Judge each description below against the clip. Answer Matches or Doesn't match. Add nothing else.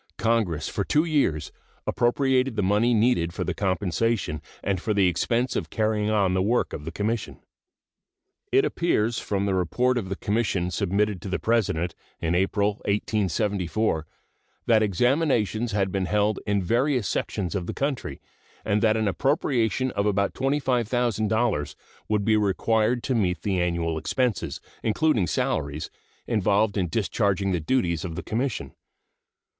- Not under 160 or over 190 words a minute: Doesn't match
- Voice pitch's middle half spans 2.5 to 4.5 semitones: Matches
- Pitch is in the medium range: Doesn't match